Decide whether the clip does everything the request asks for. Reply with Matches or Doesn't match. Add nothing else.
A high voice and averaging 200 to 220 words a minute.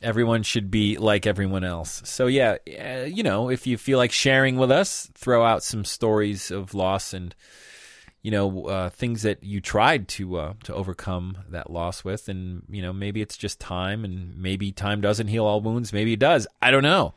Doesn't match